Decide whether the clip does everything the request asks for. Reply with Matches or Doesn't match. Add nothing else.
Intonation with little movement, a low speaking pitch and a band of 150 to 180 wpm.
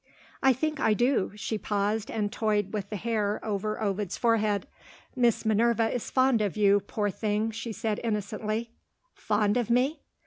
Doesn't match